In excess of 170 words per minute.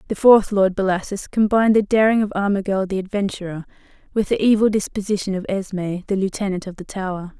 Yes: average, 180 wpm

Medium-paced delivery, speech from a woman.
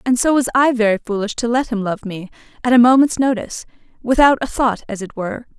No: fast, 215 wpm; female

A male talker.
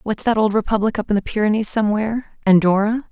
No: female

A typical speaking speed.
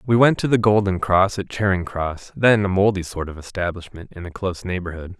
No: fast, 220 wpm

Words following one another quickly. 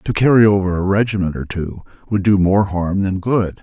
Yes: fast, 215 wpm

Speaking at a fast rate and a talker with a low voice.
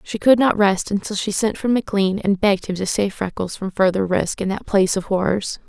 No: fast, 245 wpm; high, 200 Hz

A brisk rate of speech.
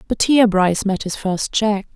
Yes: fast, 215 wpm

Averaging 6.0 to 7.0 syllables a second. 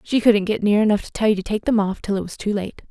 Yes: 6.6 syllables/s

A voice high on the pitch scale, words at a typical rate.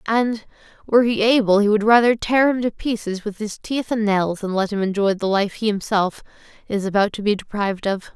No: high, 210 Hz; fast, 220 wpm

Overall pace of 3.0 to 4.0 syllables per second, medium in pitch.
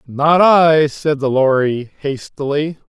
Yes: 3.4 syllables/s; medium, 145 Hz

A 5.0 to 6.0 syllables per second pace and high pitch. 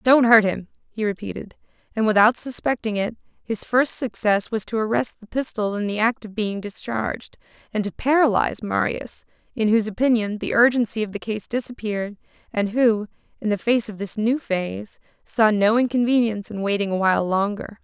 Yes: 5.4 syllables/s; high, 215 Hz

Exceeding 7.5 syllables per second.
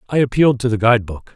Yes: 7.7 syllables/s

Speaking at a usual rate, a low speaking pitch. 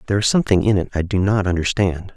No: fast, 250 wpm; very low, 95 Hz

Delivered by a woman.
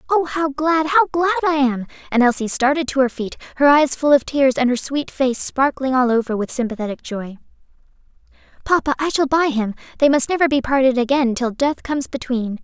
Yes: female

